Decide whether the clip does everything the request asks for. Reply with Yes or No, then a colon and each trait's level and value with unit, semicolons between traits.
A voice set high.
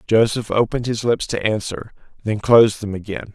No: low, 110 Hz